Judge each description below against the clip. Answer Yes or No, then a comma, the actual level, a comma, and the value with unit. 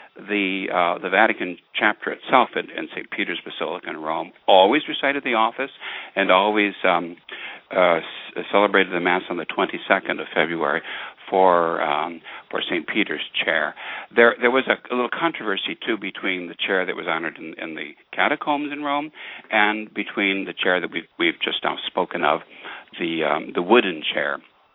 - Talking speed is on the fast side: No, average, 175 wpm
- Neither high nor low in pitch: No, low, 105 Hz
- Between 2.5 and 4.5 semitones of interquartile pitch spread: No, wide, 5.4 semitones